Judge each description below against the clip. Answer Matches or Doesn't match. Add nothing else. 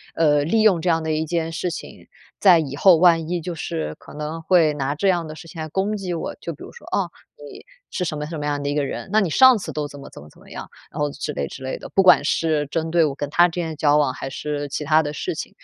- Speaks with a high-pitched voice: Doesn't match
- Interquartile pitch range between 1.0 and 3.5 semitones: Matches